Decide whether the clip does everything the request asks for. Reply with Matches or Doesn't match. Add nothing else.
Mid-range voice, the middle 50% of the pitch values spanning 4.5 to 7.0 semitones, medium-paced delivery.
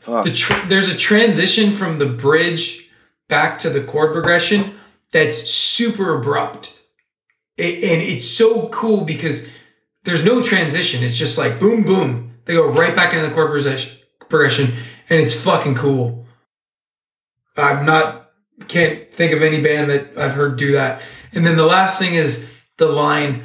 Matches